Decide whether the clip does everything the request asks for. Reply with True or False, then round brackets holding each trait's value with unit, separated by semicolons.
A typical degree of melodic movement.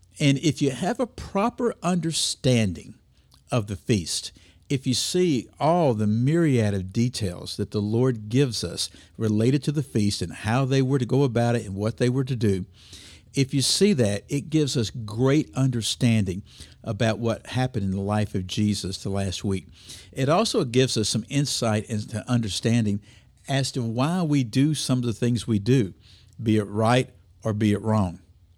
True (4.7 semitones)